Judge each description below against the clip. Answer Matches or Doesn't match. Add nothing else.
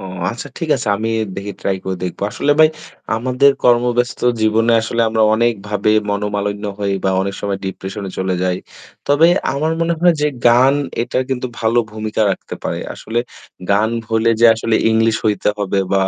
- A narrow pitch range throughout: Doesn't match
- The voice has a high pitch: Doesn't match